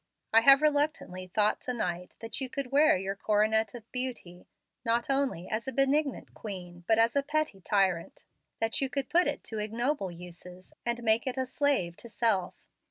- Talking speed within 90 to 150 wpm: No, average, 185 wpm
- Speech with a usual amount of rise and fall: No, wide, 5.9 semitones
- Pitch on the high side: Yes, high, 230 Hz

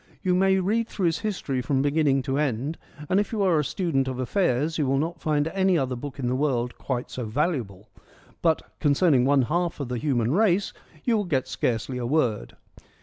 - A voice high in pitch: No, medium, 145 Hz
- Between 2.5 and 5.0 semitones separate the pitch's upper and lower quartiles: No, wide, 5.4 semitones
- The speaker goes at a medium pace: No, fast, 215 wpm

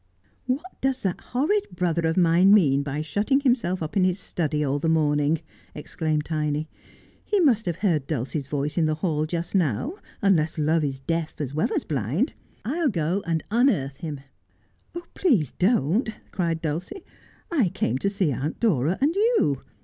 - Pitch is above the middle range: No, medium, 165 Hz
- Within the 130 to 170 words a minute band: No, average, 185 wpm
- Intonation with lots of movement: Yes, wide, 5.9 semitones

